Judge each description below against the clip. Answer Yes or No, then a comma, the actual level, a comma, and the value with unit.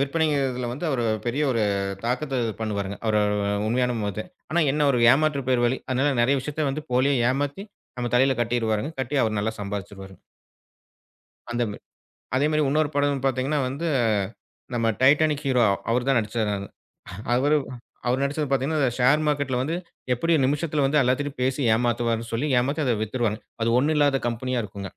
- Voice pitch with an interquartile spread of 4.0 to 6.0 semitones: No, average, 3.4 semitones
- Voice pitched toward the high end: No, low, 130 Hz